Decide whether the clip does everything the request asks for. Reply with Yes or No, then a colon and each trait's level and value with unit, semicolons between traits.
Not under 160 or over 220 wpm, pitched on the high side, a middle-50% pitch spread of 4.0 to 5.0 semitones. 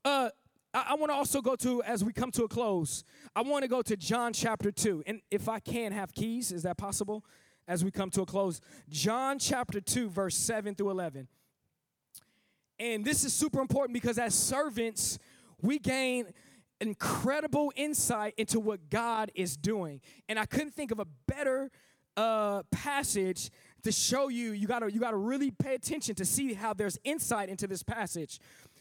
Yes: average, 185 wpm; high, 220 Hz; average, 4.4 semitones